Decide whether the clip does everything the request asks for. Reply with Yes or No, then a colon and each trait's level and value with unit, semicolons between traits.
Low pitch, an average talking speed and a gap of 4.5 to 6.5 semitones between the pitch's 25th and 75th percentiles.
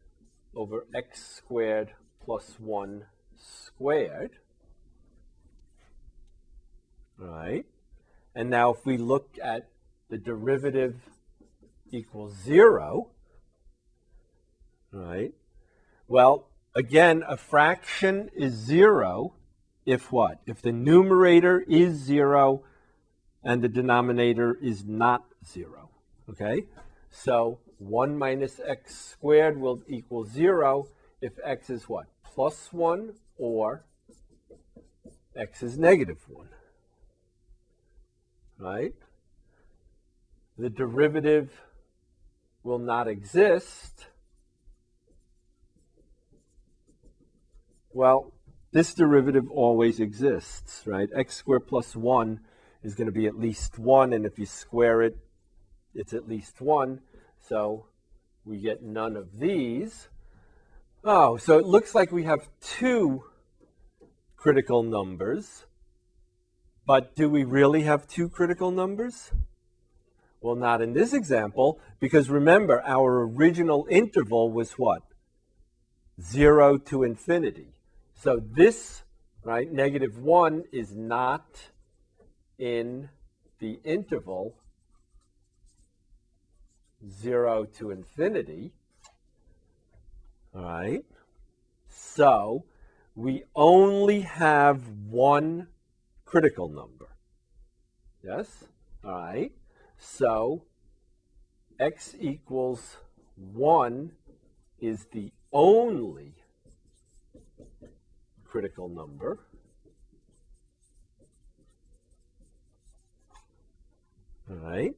No: low, 120 Hz; slow, 85 wpm; average, 5.1 semitones